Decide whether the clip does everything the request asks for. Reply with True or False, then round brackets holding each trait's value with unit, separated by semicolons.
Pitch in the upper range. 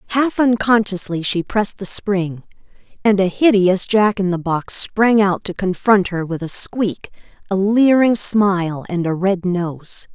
True (195 Hz)